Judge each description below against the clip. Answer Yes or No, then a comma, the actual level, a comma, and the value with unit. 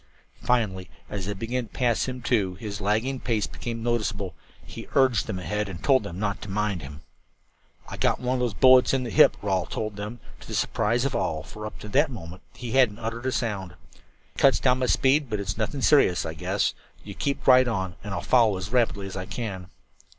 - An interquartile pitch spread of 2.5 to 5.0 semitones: Yes, average, 4.4 semitones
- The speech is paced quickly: Yes, fast, 225 wpm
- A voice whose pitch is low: Yes, low, 110 Hz